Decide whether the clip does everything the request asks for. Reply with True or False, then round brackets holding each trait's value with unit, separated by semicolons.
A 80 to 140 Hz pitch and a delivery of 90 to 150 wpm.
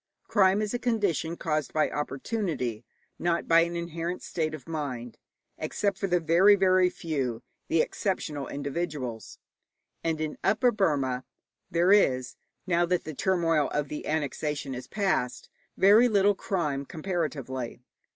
False (165 Hz; 140 wpm)